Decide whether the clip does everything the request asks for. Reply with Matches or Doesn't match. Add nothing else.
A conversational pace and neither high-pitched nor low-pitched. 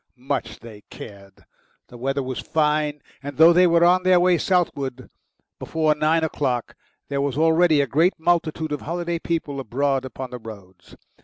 Matches